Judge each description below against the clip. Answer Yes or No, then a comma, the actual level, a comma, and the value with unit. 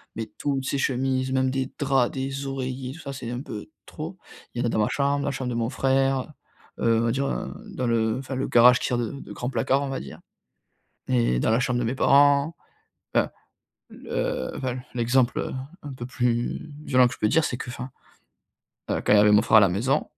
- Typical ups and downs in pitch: No, narrow, 2.3 semitones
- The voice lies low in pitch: Yes, low, 130 Hz